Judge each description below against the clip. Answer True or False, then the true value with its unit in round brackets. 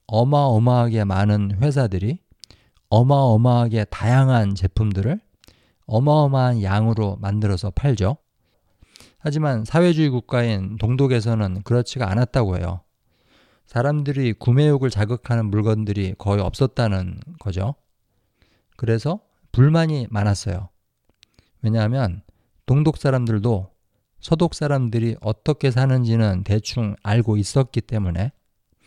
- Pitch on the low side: True (115 Hz)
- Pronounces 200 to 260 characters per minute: False (270 characters per minute)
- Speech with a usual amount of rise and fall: True (4.3 semitones)